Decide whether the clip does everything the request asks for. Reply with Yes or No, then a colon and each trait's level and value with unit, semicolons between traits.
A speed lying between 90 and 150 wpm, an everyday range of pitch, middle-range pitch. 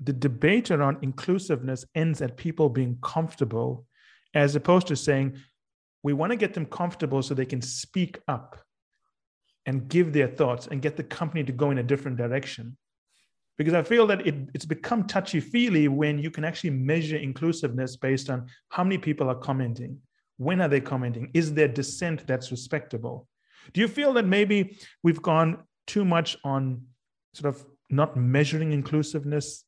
No: average, 170 wpm; average, 3.7 semitones; medium, 150 Hz